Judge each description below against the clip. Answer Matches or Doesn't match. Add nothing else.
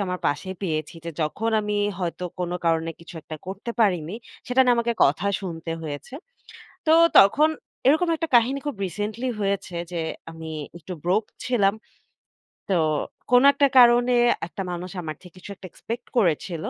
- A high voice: Matches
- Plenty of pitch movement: Matches